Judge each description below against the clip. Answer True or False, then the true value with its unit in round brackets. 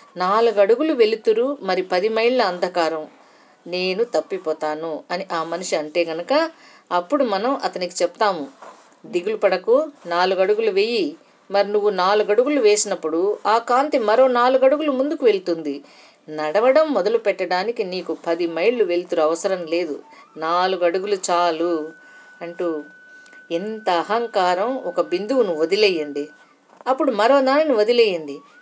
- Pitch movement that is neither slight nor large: False (8.6 semitones)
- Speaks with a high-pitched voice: True (205 Hz)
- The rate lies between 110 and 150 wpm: True (115 wpm)